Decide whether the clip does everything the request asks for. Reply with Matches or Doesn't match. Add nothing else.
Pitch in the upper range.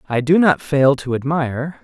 Doesn't match